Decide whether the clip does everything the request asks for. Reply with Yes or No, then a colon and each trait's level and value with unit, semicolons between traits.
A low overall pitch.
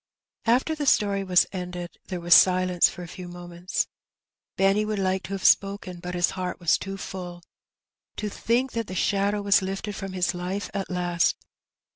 No: high, 190 Hz